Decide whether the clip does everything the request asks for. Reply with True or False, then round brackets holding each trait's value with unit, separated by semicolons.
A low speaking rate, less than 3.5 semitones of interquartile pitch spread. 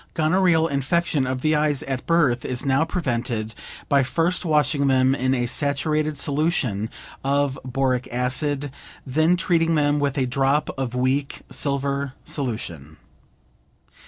True (130 wpm; 3.0 semitones)